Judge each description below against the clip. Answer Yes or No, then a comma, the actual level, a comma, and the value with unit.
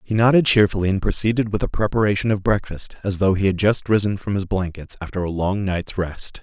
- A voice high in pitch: No, low, 100 Hz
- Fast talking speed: Yes, fast, 225 wpm